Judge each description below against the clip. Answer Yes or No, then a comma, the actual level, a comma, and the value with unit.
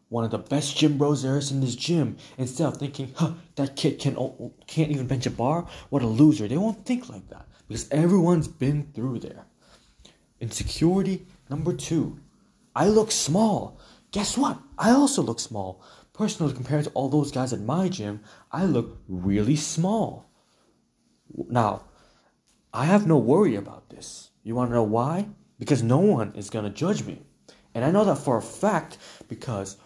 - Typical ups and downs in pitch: No, wide, 6.0 semitones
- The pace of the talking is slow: No, average, 175 wpm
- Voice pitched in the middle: Yes, medium, 145 Hz